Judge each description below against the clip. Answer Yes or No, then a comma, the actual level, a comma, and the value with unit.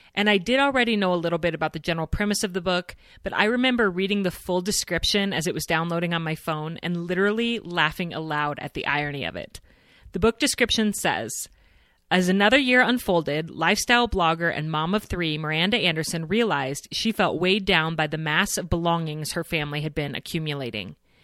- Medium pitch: Yes, medium, 170 Hz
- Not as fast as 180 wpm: No, average, 195 wpm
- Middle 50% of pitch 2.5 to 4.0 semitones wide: No, average, 4.7 semitones